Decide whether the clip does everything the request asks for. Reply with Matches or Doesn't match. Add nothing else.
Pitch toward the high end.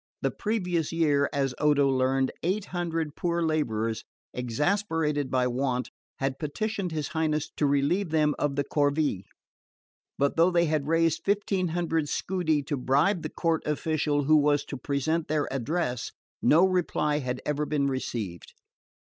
Doesn't match